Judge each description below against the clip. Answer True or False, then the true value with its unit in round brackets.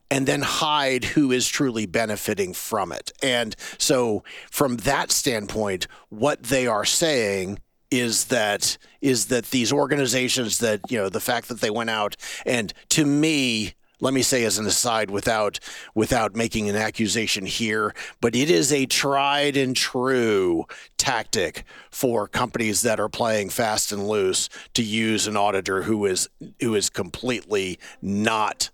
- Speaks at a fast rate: False (155 wpm)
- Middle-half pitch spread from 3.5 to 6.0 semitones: True (4.0 semitones)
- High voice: False (115 Hz)